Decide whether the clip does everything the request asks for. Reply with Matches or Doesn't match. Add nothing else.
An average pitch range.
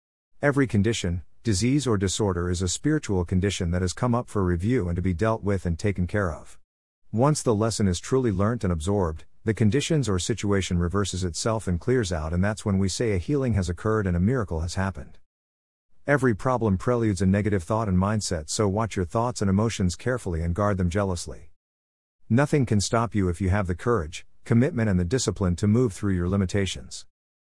Matches